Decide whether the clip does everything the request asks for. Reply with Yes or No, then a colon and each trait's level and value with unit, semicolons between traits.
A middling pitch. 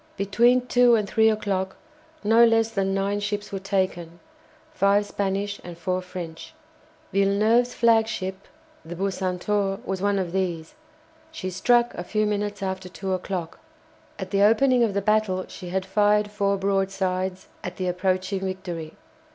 No: high, 195 Hz